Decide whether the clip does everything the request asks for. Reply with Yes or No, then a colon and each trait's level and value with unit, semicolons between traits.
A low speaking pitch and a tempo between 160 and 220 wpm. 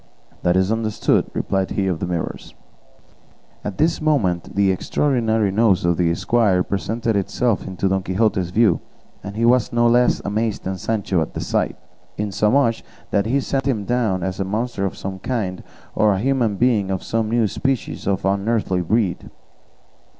Yes: low, 105 Hz; average, 170 wpm